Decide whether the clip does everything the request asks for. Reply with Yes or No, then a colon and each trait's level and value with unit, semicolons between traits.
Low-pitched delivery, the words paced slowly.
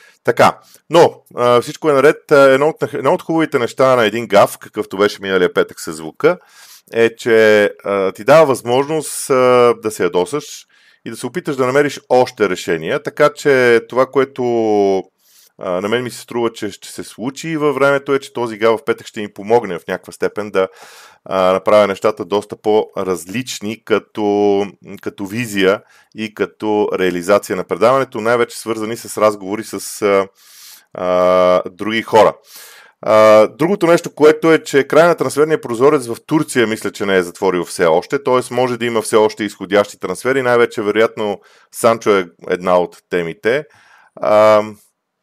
No: low, 115 Hz; average, 160 wpm